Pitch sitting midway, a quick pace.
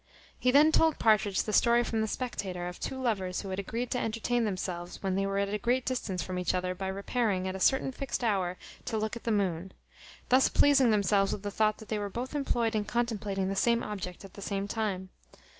No: high, 210 Hz; fast, 230 wpm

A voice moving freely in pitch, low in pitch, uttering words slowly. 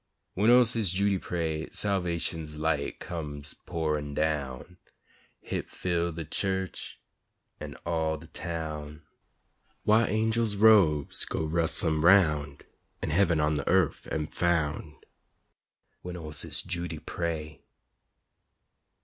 No: average, 3.2 semitones; very low, 80 Hz; slow, 115 wpm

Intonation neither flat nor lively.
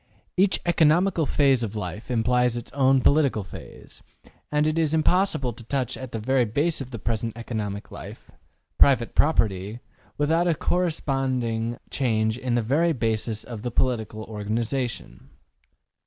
Yes: average, 4.6 semitones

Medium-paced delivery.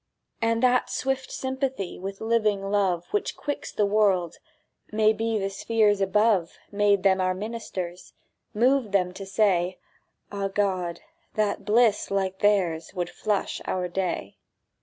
No: slow, 130 wpm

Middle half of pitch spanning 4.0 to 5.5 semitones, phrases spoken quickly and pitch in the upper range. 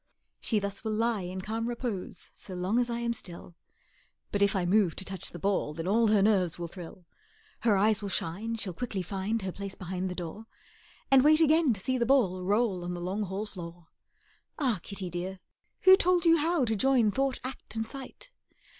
Yes: average, 4.3 semitones; fast, 210 wpm; high, 205 Hz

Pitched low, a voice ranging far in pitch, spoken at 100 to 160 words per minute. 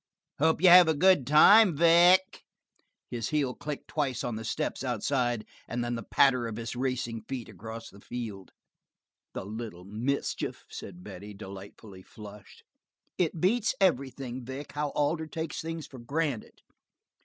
Yes: low, 130 Hz; wide, 5.8 semitones; average, 150 wpm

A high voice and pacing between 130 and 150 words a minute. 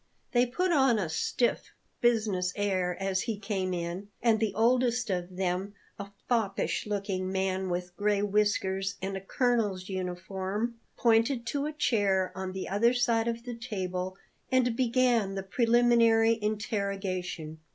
Yes: high, 205 Hz; average, 145 wpm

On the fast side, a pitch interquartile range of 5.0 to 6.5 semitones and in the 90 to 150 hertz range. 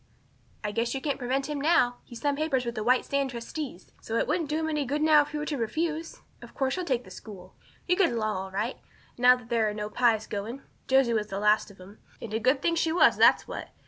No: fast, 260 wpm; wide, 5.4 semitones; very high, 250 Hz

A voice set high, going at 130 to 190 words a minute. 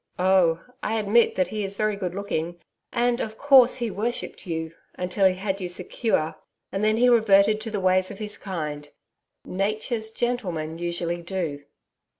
Yes: high, 195 Hz; average, 165 wpm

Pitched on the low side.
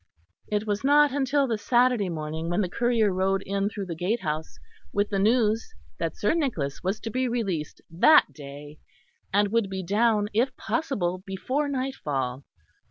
No: high, 205 Hz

